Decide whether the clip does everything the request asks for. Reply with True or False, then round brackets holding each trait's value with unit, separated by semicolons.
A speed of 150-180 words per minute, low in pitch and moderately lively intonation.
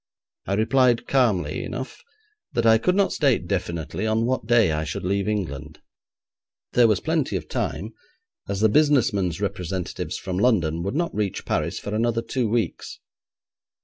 True (160 wpm; 110 Hz; 5.0 semitones)